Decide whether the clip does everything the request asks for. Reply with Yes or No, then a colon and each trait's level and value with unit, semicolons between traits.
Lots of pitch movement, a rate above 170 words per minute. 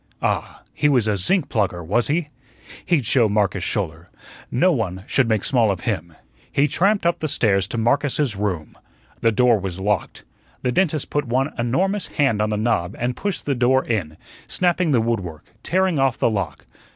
Yes: wide, 6.4 semitones; average, 190 wpm